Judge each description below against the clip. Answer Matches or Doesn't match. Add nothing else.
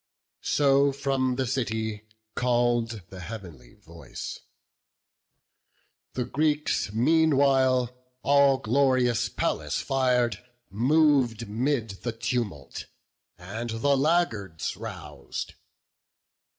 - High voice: Doesn't match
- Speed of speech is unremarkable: Doesn't match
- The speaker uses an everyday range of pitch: Matches